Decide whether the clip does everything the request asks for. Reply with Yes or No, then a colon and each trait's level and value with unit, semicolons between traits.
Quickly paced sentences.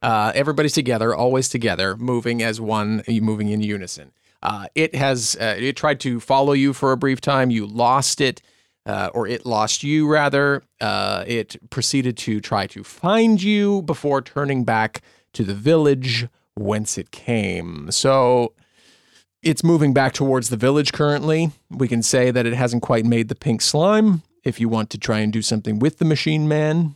No: average, 180 wpm